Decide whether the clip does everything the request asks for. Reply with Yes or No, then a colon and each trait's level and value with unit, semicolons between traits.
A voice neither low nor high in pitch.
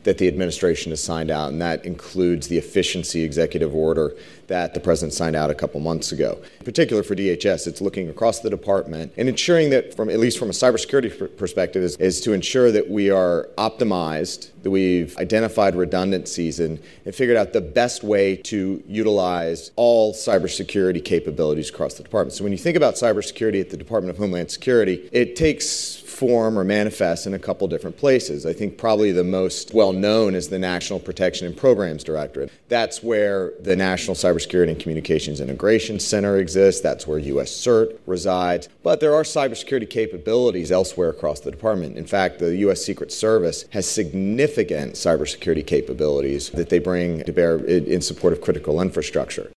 No: very low, 95 Hz